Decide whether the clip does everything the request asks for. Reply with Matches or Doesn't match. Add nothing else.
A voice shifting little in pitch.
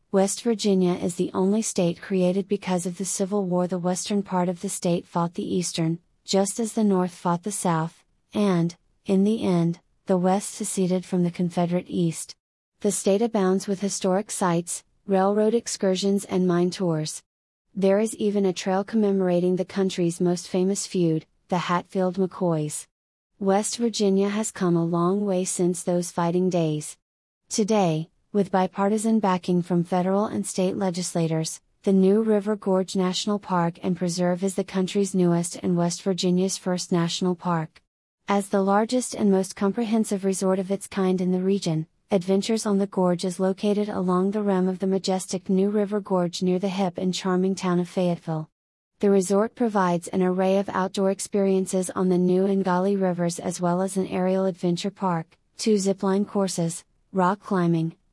Matches